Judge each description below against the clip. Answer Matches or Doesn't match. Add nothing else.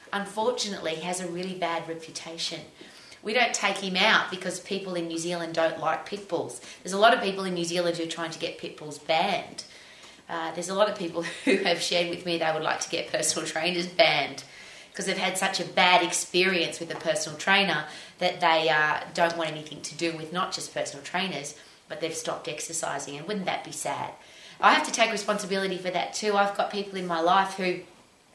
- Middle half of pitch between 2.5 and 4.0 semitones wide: Matches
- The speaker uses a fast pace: Matches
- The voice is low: Doesn't match